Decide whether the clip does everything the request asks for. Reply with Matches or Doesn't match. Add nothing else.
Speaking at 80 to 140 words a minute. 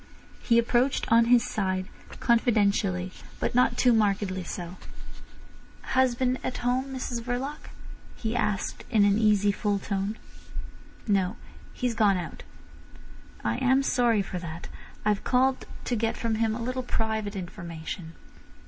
Matches